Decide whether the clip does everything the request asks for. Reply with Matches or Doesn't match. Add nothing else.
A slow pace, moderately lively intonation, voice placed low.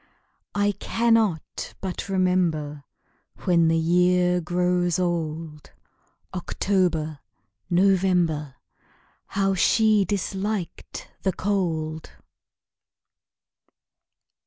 Doesn't match